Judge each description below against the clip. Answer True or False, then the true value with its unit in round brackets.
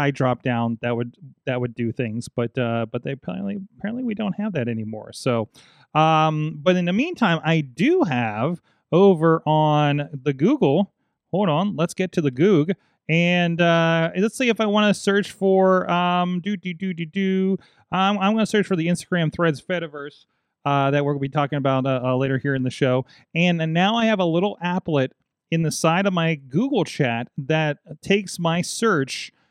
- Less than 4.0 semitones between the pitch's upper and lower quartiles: False (5.4 semitones)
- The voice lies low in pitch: False (165 Hz)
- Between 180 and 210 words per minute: True (200 wpm)